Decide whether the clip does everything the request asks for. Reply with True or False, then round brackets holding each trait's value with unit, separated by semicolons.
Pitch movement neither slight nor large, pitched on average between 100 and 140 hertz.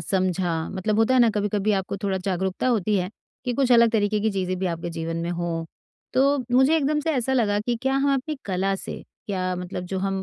False (4.9 semitones; 200 Hz)